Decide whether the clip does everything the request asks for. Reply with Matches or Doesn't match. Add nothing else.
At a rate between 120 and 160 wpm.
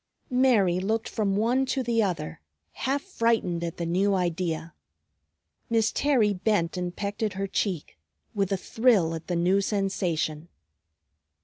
Matches